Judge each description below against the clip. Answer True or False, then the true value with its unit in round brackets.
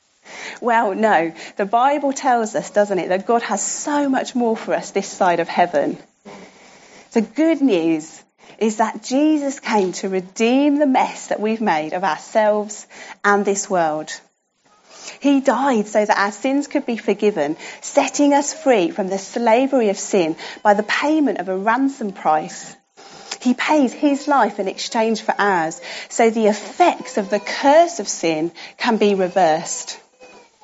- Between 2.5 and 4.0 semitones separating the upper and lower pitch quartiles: False (5.4 semitones)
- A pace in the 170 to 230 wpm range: False (160 wpm)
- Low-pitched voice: False (220 Hz)